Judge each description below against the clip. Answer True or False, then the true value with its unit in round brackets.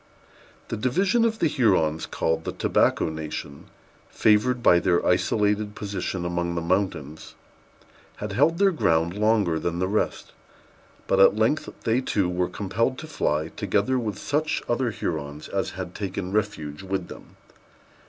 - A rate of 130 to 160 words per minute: True (145 wpm)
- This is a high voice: False (100 Hz)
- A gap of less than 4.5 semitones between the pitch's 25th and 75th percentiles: False (5.1 semitones)